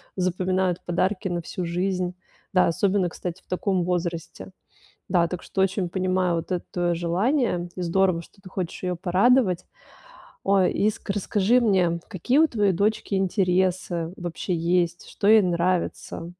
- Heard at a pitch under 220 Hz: Yes, medium, 185 Hz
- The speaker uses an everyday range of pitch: No, narrow, 1.9 semitones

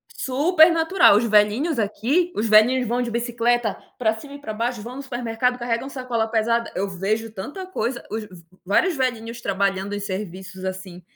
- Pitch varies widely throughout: No, average, 3.6 semitones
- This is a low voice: No, high, 230 Hz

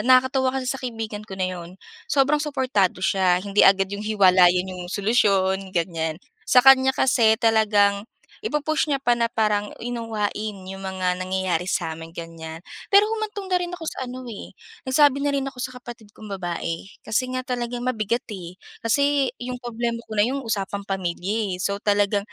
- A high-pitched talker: Yes, high, 215 Hz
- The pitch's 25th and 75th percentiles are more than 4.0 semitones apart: Yes, average, 5.1 semitones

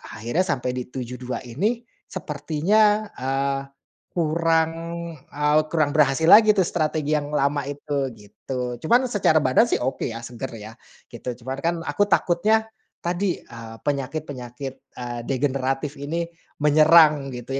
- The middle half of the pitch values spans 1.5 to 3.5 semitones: No, average, 4.4 semitones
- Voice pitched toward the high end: No, medium, 145 Hz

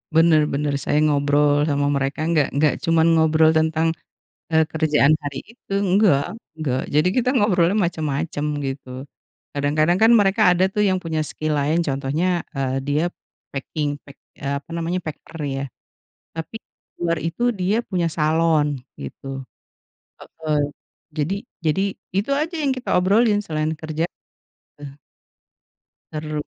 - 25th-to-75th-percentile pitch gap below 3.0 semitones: No, average, 3.6 semitones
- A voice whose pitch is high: No, medium, 160 Hz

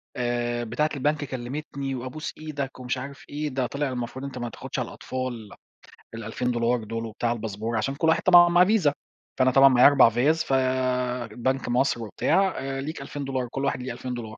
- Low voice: Yes, low, 130 Hz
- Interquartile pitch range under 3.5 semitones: Yes, average, 3.0 semitones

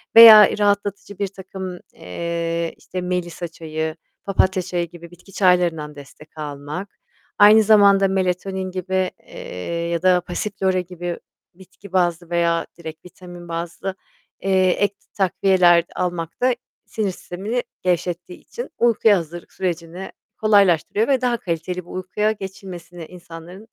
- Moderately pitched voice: Yes, medium, 180 Hz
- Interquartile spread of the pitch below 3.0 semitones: Yes, narrow, 2.4 semitones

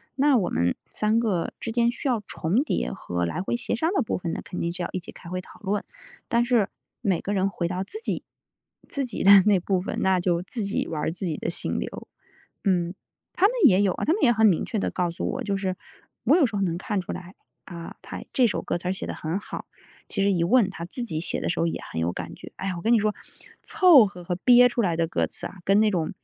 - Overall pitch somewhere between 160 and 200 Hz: Yes, high, 195 Hz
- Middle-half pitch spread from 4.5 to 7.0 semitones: Yes, average, 4.9 semitones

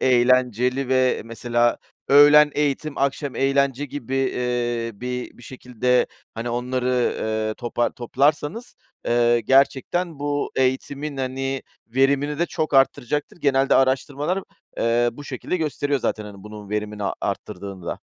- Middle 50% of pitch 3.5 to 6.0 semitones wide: No, average, 3.0 semitones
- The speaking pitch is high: No, low, 130 Hz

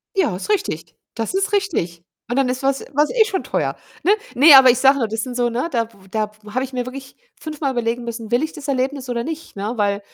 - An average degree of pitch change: Yes, average, 4.1 semitones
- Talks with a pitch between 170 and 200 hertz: No, very high, 255 Hz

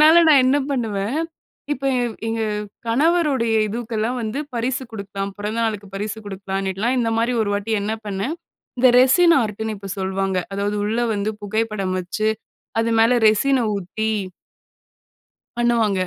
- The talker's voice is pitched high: Yes, high, 220 Hz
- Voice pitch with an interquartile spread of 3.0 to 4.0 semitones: Yes, average, 3.6 semitones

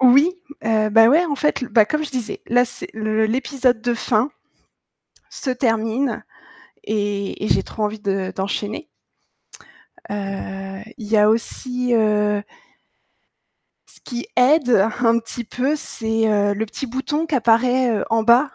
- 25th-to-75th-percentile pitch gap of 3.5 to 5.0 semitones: No, average, 3.1 semitones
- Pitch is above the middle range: Yes, high, 230 Hz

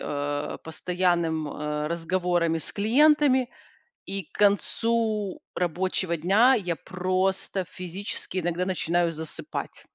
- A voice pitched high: No, medium, 180 Hz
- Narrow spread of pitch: No, average, 3.3 semitones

